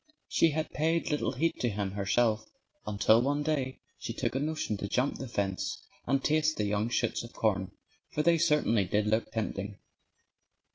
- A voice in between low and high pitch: No, low, 120 Hz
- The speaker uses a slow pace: No, average, 180 wpm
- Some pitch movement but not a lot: No, wide, 6.4 semitones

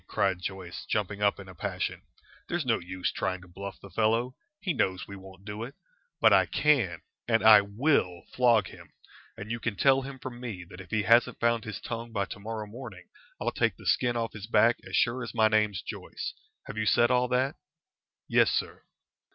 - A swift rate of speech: Yes, fast, 210 wpm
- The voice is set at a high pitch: No, low, 110 Hz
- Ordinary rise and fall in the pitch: Yes, average, 3.5 semitones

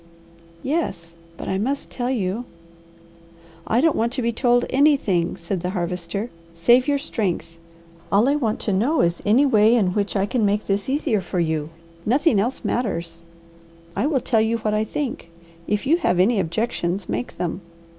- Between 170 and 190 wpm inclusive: Yes, average, 180 wpm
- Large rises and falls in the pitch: Yes, wide, 5.9 semitones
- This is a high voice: Yes, high, 210 Hz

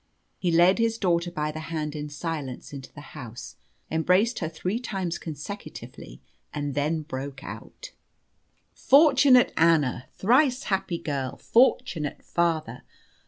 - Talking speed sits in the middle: No, slow, 125 wpm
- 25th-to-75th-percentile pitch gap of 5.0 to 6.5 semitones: Yes, wide, 5.4 semitones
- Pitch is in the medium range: Yes, medium, 165 Hz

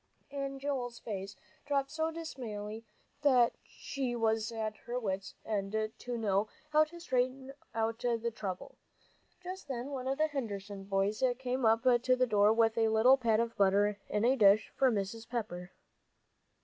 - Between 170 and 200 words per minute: No, average, 160 wpm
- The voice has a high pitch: Yes, high, 230 Hz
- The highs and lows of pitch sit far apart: No, average, 3.8 semitones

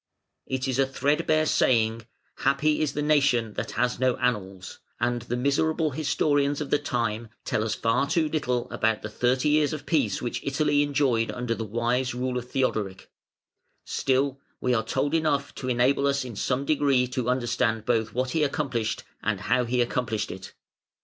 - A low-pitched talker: Yes, low, 125 Hz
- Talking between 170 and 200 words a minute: Yes, average, 175 wpm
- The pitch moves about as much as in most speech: Yes, average, 3.4 semitones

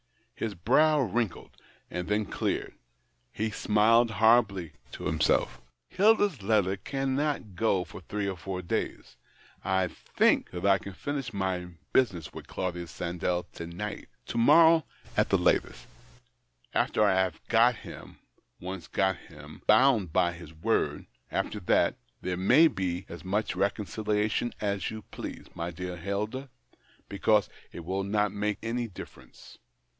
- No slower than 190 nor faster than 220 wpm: No, average, 150 wpm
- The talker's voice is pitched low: Yes, low, 100 Hz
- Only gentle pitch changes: No, average, 4.0 semitones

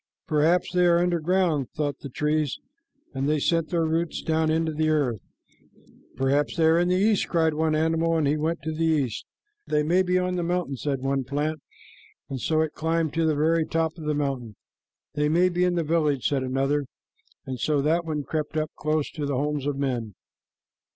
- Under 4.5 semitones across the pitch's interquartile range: Yes, narrow, 2.5 semitones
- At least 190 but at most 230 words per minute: Yes, fast, 205 wpm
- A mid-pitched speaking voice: Yes, medium, 155 Hz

